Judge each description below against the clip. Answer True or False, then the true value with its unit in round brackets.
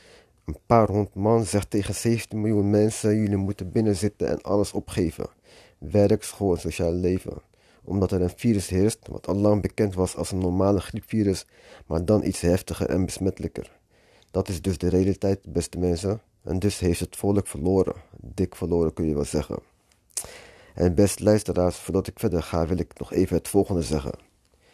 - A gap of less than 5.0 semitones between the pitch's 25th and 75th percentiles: True (2.8 semitones)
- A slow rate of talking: False (175 wpm)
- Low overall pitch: True (95 Hz)